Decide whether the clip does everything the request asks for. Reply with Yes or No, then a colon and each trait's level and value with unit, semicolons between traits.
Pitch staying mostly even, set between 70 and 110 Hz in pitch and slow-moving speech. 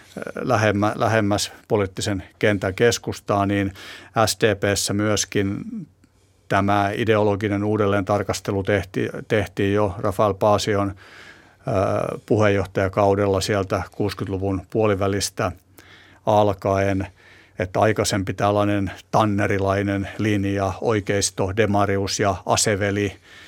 Yes: narrow, 1.3 semitones; low, 100 Hz; slow, 80 wpm